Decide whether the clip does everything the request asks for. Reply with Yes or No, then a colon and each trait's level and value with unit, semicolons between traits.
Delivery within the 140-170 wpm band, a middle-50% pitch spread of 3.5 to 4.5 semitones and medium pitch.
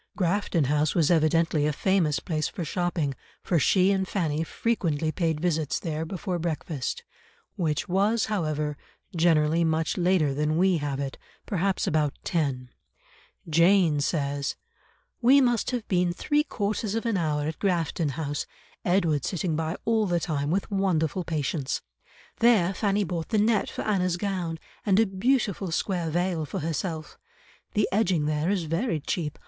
Yes: average, 155 wpm; average, 4.0 semitones; medium, 170 Hz